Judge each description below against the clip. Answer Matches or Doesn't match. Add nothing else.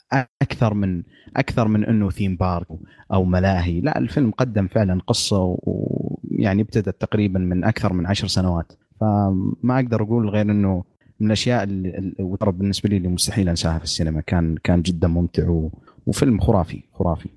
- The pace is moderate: Doesn't match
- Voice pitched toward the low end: Matches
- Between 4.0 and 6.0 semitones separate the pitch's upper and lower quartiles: Doesn't match